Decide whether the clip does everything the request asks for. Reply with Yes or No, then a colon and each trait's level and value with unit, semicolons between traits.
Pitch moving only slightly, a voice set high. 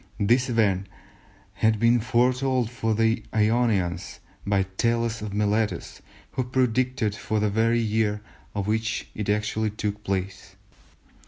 No: narrow, 2.1 semitones; low, 110 Hz